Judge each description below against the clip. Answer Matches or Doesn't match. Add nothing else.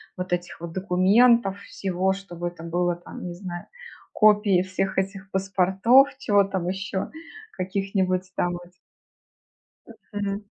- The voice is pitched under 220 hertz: Matches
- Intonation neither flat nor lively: Doesn't match